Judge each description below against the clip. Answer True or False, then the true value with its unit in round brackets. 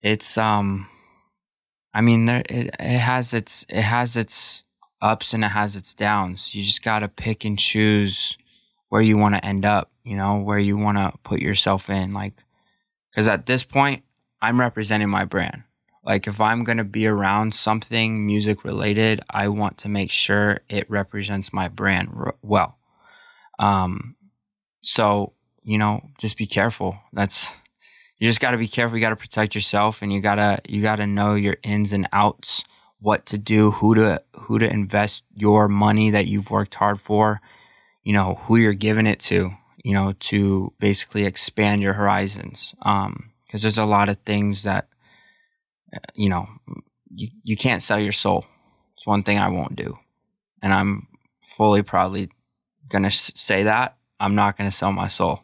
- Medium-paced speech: True (180 wpm)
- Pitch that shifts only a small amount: True (1.7 semitones)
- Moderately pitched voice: False (105 Hz)